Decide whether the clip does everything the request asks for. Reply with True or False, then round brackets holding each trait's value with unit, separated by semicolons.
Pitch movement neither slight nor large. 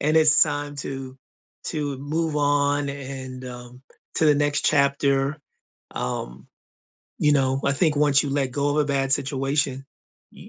False (1.5 semitones)